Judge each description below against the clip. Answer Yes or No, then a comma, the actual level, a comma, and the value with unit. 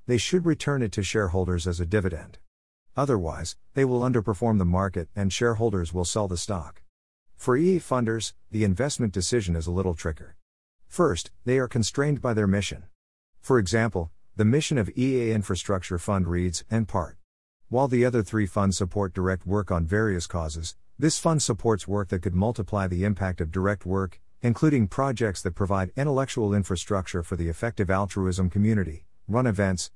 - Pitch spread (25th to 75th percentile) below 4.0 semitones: No, average, 4.5 semitones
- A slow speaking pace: No, average, 170 wpm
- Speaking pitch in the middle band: No, low, 100 Hz